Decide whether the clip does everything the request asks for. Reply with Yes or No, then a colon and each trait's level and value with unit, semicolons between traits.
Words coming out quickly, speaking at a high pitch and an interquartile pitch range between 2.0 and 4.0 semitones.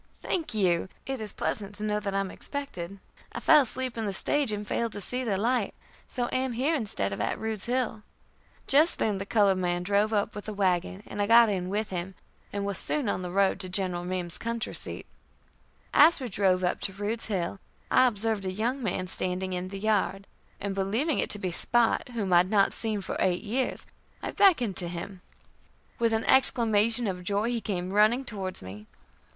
Yes: fast, 210 wpm; high, 205 Hz; average, 3.7 semitones